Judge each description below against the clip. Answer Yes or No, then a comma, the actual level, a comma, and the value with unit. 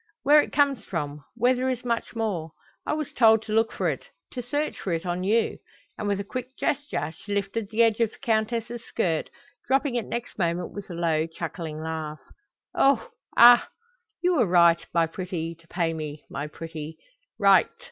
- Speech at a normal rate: Yes, average, 190 wpm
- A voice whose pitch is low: No, high, 200 Hz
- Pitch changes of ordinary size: No, wide, 6.3 semitones